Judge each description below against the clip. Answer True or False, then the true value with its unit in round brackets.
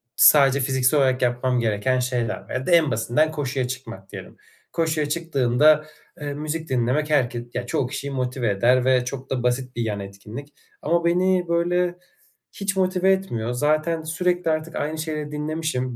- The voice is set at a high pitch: False (140 Hz)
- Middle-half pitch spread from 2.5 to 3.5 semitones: False (4.3 semitones)